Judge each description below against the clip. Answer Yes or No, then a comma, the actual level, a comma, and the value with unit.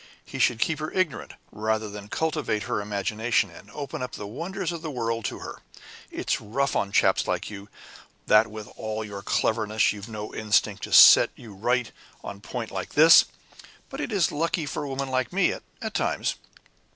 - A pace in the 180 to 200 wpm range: Yes, average, 190 wpm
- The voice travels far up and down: Yes, wide, 5.7 semitones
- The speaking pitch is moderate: No, low, 115 Hz